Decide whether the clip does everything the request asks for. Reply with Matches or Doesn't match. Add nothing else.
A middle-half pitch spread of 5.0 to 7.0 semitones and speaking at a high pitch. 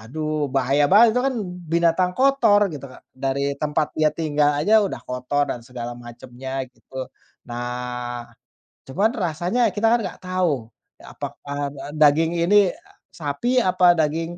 Doesn't match